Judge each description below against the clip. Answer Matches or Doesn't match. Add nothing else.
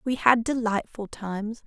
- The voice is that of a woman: Matches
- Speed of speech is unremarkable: Matches